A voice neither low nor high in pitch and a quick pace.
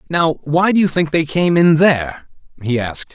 Yes: medium, 155 Hz; fast, 210 wpm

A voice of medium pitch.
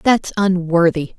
Yes: medium, 180 Hz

